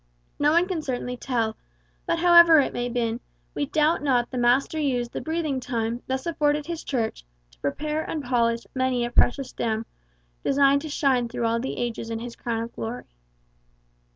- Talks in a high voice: Yes, very high, 255 Hz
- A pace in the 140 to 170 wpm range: No, average, 180 wpm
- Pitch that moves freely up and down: No, average, 4.0 semitones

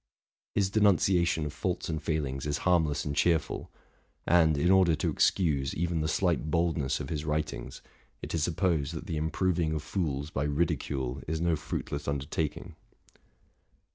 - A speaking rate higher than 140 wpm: Yes, average, 155 wpm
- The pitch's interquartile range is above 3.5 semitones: No, average, 2.9 semitones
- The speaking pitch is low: Yes, very low, 80 Hz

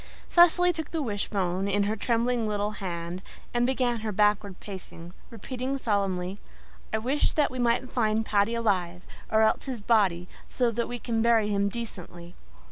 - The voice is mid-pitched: No, high, 215 Hz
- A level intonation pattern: No, average, 3.3 semitones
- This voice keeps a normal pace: Yes, average, 165 wpm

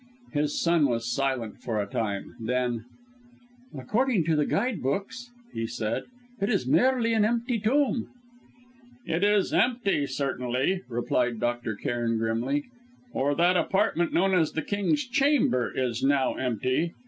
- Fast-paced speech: No, average, 140 wpm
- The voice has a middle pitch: Yes, medium, 145 Hz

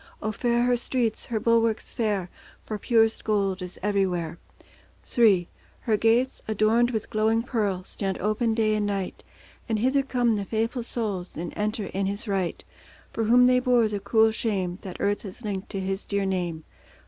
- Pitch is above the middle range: Yes, high, 215 Hz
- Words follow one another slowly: No, average, 175 wpm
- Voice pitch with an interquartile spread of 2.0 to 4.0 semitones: Yes, average, 2.9 semitones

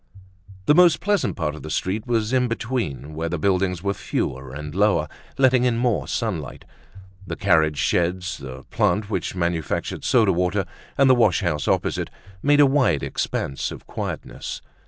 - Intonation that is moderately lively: No, wide, 7.3 semitones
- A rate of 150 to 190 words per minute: Yes, average, 165 wpm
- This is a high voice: No, very low, 95 Hz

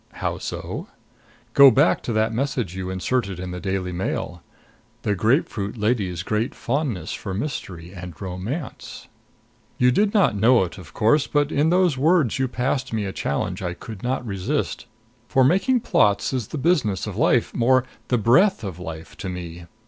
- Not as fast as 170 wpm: No, average, 175 wpm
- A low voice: Yes, low, 110 Hz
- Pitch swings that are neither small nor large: No, wide, 6.1 semitones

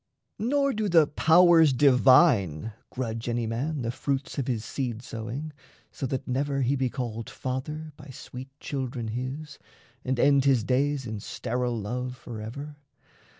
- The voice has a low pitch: Yes, low, 130 Hz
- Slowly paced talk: No, average, 150 wpm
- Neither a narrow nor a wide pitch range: Yes, average, 3.4 semitones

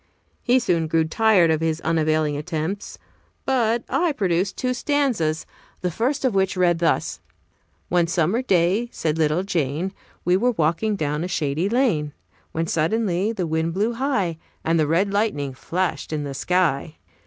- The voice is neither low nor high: Yes, medium, 175 Hz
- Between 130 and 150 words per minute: No, average, 160 wpm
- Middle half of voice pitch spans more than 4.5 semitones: Yes, wide, 5.4 semitones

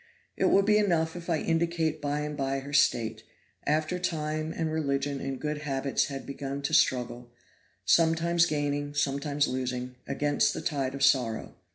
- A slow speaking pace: No, average, 165 wpm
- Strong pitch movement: No, average, 2.8 semitones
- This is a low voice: No, medium, 145 Hz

